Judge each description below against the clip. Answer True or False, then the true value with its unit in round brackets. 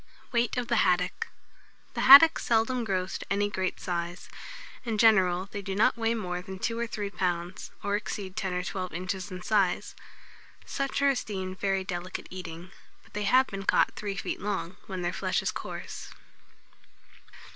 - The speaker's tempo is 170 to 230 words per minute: True (175 wpm)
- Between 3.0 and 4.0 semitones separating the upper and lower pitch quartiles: True (3.3 semitones)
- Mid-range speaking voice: False (195 Hz)